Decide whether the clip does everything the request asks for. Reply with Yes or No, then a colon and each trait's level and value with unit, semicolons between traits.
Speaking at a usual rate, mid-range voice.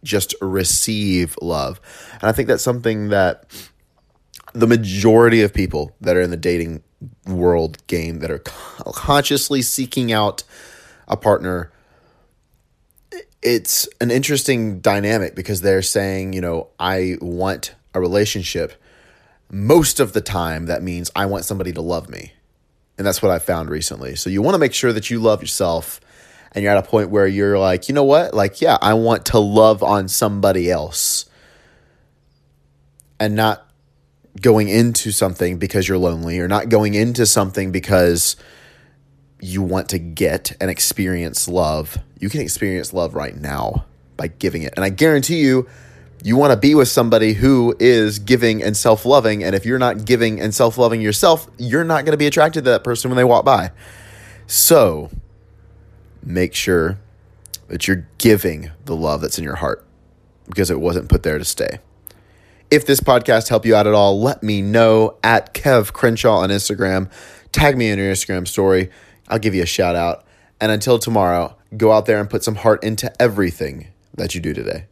No: average, 175 wpm; low, 100 Hz